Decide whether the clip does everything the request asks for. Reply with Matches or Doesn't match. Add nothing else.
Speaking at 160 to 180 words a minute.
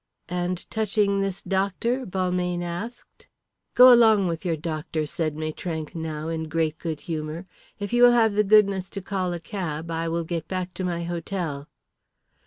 Matches